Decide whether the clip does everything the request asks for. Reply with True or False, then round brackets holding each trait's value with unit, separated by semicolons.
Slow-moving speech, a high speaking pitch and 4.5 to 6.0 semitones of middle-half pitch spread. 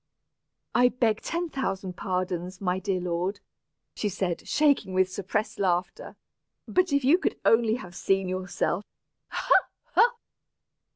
True (130 wpm; 195 Hz; 5.2 semitones)